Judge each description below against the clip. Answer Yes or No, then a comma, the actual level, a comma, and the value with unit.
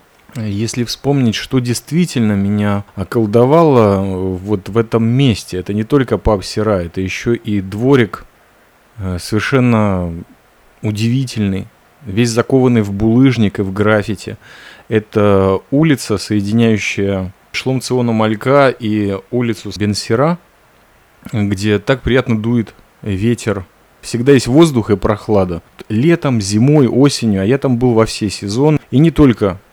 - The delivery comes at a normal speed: Yes, average, 120 wpm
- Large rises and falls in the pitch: No, average, 3.5 semitones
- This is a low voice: Yes, low, 110 Hz